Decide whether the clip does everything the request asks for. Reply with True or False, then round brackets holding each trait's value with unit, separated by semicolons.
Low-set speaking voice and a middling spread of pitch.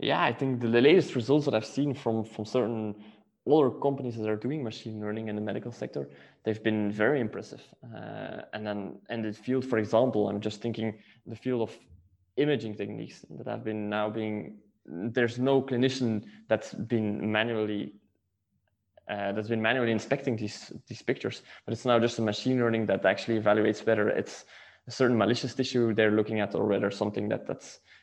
False (110 Hz; 2.3 semitones)